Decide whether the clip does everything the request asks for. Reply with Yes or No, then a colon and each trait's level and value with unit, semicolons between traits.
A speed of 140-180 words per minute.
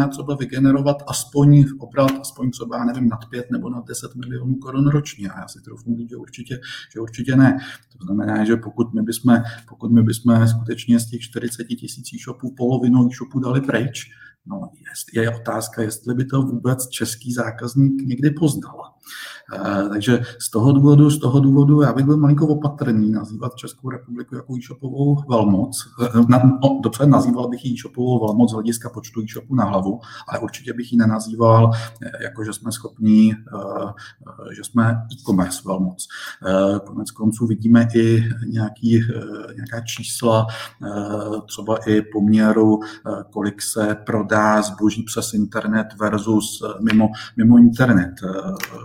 Yes: average, 150 wpm